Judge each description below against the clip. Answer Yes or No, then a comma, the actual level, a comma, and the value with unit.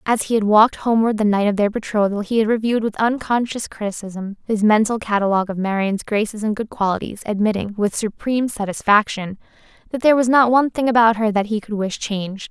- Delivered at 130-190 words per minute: No, average, 200 wpm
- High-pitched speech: Yes, high, 215 Hz